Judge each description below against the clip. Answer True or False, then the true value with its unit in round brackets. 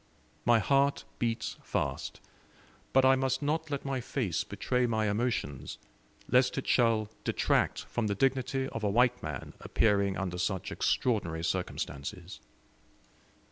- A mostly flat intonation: False (4.9 semitones)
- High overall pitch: False (115 Hz)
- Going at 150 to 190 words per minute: False (135 wpm)